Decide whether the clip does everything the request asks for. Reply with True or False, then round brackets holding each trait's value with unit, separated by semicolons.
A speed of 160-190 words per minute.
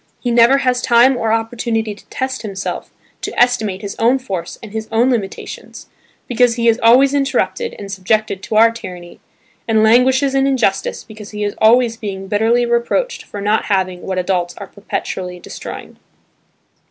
True (165 wpm)